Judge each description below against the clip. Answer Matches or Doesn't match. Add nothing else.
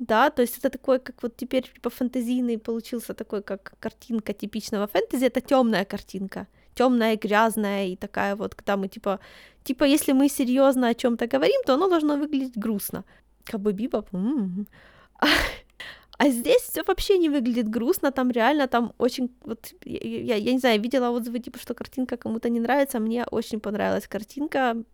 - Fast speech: Matches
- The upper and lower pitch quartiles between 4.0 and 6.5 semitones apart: Doesn't match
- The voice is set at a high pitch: Matches